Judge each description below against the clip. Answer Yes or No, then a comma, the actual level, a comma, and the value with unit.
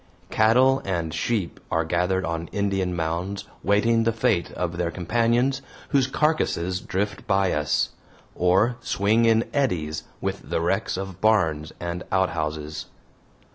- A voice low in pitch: Yes, very low, 95 Hz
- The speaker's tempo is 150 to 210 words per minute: No, slow, 135 wpm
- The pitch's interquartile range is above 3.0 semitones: Yes, average, 5.1 semitones